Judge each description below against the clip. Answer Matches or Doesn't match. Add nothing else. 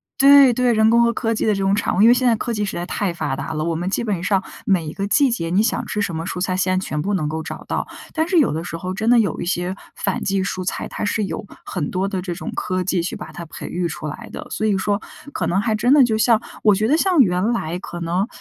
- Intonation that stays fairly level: Doesn't match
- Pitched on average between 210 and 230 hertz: Doesn't match